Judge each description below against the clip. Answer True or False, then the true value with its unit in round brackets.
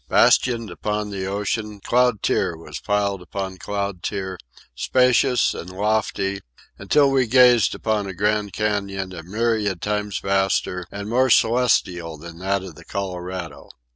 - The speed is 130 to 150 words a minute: True (140 wpm)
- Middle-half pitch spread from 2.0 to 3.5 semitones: True (2.7 semitones)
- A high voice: False (100 Hz)